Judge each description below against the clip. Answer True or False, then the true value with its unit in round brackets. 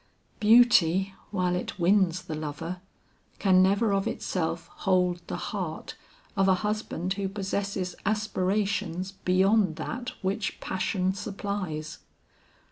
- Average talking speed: False (115 wpm)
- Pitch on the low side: False (190 Hz)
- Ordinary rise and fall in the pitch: False (2.1 semitones)